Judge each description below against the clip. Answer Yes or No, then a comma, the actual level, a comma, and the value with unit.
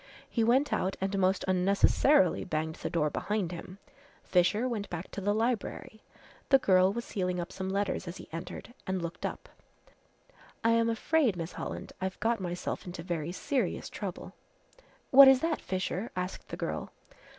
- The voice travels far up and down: No, average, 4.3 semitones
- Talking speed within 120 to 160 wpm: No, average, 170 wpm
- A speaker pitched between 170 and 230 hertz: Yes, high, 190 Hz